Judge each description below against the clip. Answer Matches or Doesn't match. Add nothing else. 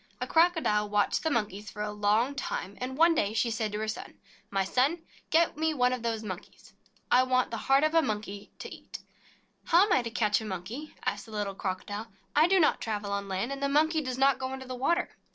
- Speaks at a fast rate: Matches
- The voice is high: Matches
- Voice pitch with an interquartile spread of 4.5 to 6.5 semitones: Matches